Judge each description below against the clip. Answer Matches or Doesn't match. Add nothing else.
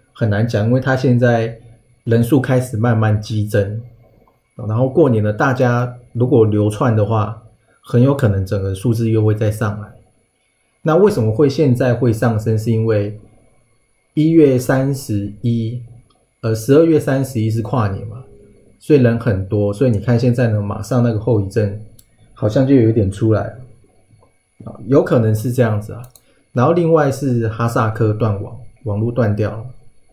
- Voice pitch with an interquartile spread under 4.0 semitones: Matches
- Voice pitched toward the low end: Matches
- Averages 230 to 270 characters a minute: Matches